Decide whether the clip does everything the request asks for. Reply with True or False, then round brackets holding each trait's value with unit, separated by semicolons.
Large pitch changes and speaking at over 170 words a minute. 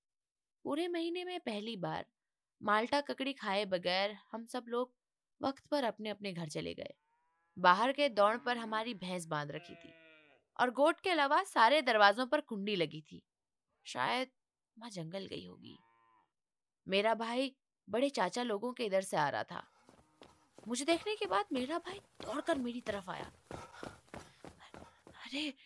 False (6.2 semitones; 150 wpm)